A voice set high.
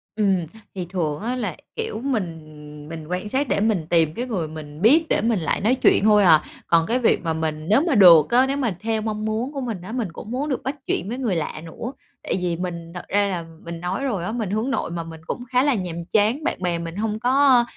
Yes: high, 205 Hz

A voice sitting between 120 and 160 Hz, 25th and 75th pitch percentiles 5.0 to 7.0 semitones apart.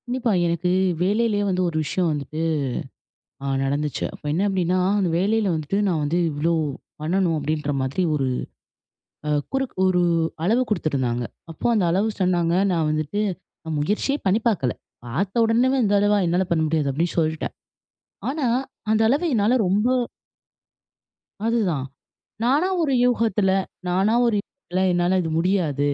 No: medium, 185 Hz; average, 5.3 semitones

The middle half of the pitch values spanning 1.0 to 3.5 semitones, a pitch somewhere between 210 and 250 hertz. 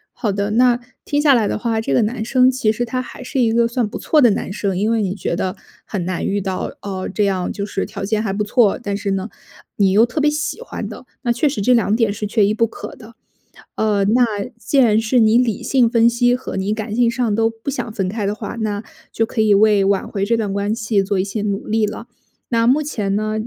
Yes: average, 2.9 semitones; high, 220 Hz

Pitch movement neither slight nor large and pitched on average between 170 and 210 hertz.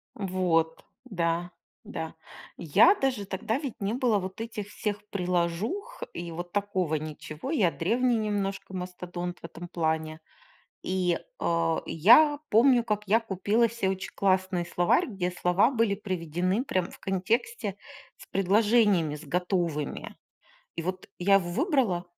Yes: average, 4.0 semitones; high, 190 Hz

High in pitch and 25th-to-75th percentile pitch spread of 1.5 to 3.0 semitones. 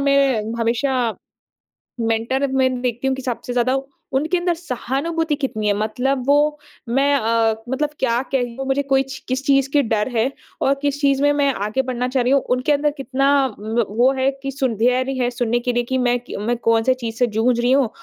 Yes: very high, 255 Hz; narrow, 2.5 semitones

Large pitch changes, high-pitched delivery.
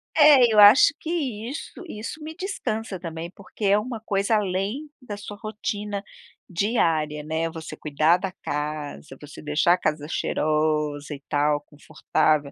No: wide, 5.8 semitones; medium, 180 Hz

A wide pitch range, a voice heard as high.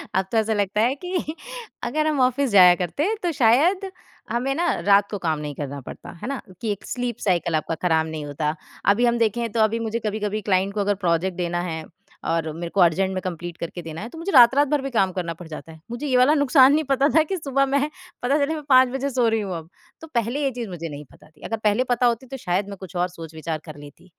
Yes: wide, 7.3 semitones; high, 215 Hz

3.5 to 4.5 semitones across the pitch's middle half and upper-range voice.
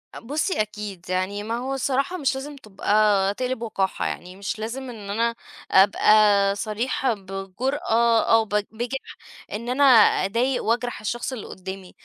Yes: average, 4.2 semitones; high, 230 Hz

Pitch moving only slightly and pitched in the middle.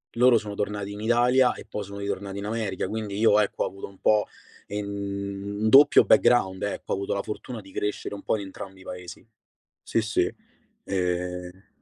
No: narrow, 1.8 semitones; low, 100 Hz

